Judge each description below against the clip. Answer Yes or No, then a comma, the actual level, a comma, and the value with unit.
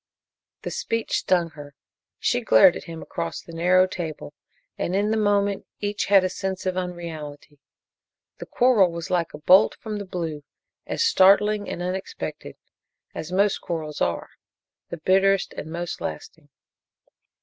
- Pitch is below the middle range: No, medium, 180 Hz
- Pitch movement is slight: No, average, 3.4 semitones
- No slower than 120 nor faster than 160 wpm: Yes, average, 150 wpm